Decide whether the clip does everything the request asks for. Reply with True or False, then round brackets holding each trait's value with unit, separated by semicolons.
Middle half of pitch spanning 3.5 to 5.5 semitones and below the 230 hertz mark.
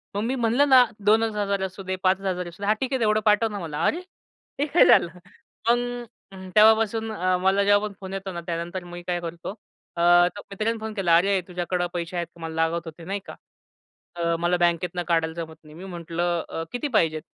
True (3.8 semitones; 190 Hz)